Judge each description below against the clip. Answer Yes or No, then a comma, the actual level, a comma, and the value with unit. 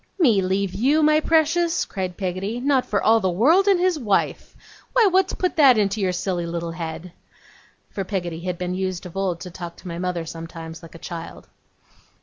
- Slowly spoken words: No, average, 195 wpm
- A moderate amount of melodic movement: No, wide, 7.7 semitones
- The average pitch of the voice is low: No, high, 190 Hz